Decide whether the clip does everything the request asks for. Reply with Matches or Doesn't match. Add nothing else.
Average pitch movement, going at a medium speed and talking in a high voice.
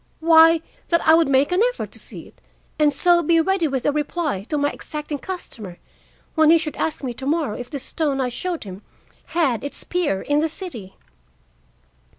Matches